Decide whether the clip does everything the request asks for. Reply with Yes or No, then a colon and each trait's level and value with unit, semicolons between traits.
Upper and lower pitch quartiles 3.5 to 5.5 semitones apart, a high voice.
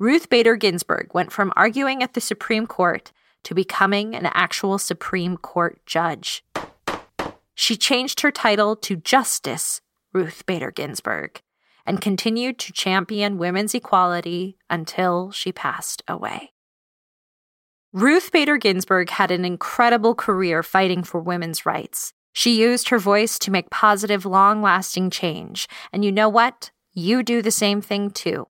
Yes: average, 4.0 semitones; high, 200 Hz